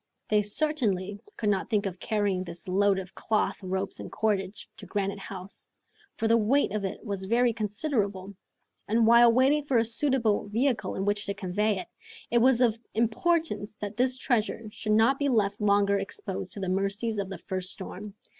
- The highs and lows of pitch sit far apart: No, average, 2.9 semitones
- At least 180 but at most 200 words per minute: Yes, average, 185 wpm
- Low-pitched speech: No, high, 210 Hz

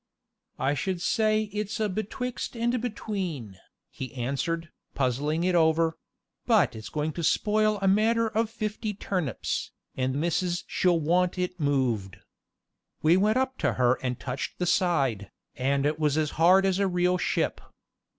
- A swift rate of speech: No, average, 155 wpm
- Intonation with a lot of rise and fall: Yes, wide, 6.8 semitones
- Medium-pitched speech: Yes, medium, 175 Hz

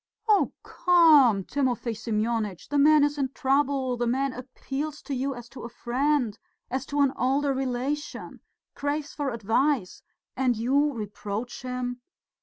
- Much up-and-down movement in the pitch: No, average, 3.1 semitones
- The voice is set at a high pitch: Yes, very high, 260 Hz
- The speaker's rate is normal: Yes, average, 145 wpm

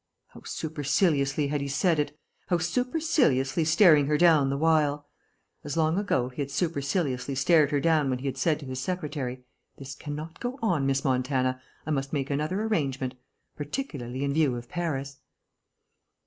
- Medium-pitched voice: Yes, medium, 145 Hz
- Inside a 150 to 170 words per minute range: Yes, average, 165 wpm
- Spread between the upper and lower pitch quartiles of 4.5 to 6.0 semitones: No, average, 3.2 semitones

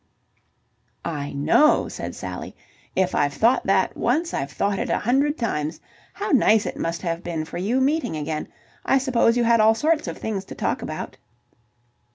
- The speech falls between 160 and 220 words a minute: Yes, average, 180 wpm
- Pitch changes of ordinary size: No, wide, 7.9 semitones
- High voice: Yes, high, 215 Hz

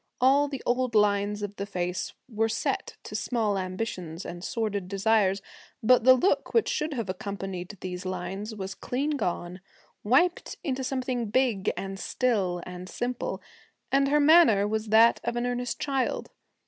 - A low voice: No, high, 215 Hz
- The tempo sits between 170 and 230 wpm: No, average, 160 wpm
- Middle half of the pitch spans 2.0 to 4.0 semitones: No, average, 4.7 semitones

